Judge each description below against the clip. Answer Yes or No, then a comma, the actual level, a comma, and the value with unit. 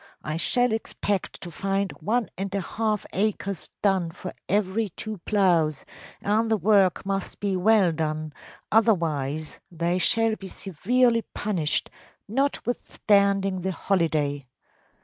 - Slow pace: Yes, slow, 125 wpm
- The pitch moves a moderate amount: Yes, average, 4.1 semitones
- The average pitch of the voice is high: Yes, high, 195 Hz